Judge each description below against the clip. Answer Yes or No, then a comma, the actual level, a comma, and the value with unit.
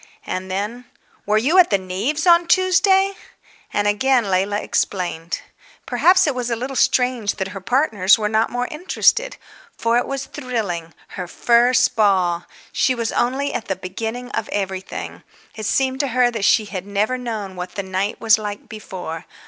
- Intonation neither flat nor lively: Yes, average, 4.8 semitones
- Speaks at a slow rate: No, average, 175 wpm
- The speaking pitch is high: Yes, high, 220 Hz